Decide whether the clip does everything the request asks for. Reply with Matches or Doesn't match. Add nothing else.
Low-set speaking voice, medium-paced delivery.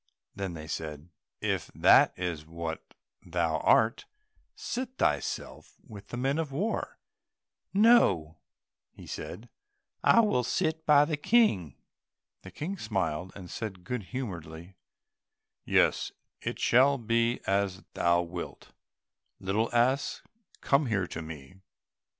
Doesn't match